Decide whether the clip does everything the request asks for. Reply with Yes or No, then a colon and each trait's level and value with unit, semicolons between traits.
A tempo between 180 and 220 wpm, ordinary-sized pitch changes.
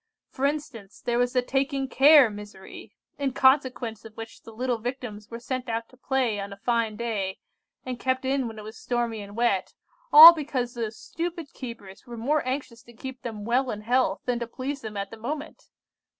Yes: average, 200 wpm; average, 3.0 semitones